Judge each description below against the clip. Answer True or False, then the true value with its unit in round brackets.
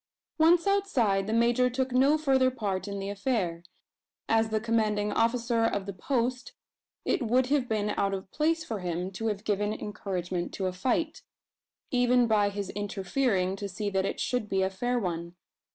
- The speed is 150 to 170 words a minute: False (180 wpm)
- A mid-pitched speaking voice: False (215 Hz)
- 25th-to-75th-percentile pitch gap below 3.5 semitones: False (4.2 semitones)